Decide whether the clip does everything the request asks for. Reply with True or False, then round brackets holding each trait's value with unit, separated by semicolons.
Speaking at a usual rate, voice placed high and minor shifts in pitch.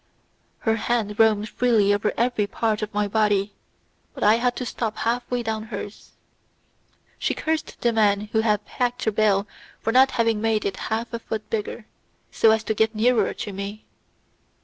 True (180 wpm; 220 Hz; 1.8 semitones)